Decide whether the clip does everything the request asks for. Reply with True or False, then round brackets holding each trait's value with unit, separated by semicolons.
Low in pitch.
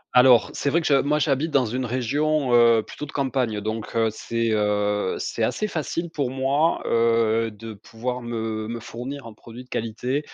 True (120 Hz)